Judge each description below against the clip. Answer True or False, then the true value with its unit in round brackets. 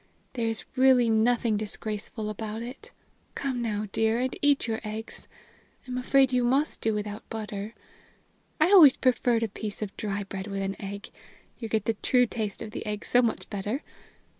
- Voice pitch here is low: False (225 Hz)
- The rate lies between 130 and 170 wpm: False (180 wpm)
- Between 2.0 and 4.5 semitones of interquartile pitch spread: True (2.9 semitones)